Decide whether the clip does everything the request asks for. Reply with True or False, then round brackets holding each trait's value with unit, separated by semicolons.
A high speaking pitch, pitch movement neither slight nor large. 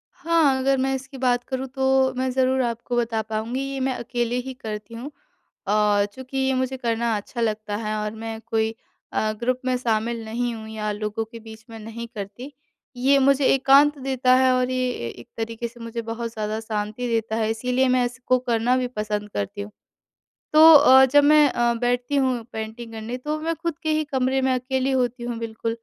True (245 Hz; 3.0 semitones)